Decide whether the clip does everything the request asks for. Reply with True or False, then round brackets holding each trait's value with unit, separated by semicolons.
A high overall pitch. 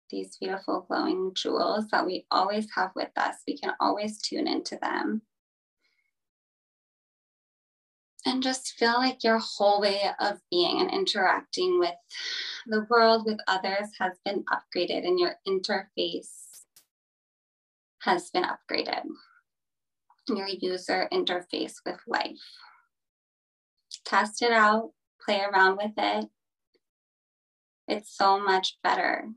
True (235 Hz)